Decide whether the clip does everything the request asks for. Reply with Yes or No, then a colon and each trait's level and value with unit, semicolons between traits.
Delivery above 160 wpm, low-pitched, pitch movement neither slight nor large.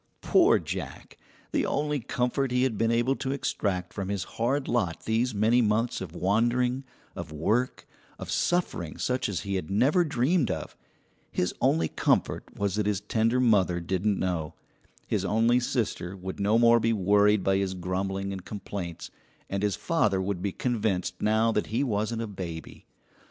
Yes: average, 170 wpm; low, 105 Hz; average, 4.1 semitones